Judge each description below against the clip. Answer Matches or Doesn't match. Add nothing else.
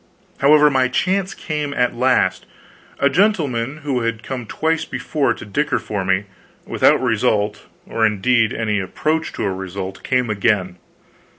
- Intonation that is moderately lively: Doesn't match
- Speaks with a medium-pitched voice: Doesn't match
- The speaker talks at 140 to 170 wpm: Matches